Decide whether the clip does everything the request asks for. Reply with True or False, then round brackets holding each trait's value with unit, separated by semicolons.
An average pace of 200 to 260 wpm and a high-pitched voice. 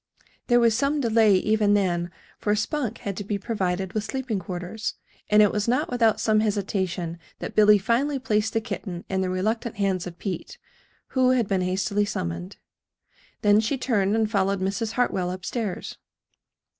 False (170 wpm; 210 Hz)